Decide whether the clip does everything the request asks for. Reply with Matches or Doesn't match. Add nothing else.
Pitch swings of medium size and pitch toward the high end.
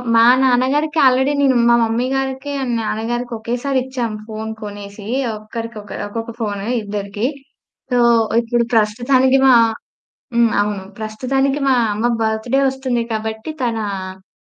Matches